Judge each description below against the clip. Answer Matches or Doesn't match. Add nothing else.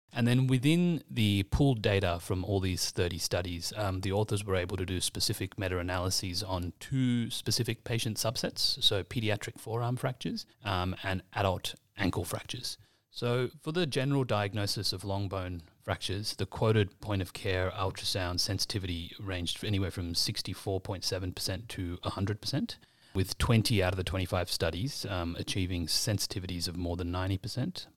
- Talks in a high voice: Doesn't match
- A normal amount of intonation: Matches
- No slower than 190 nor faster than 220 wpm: Doesn't match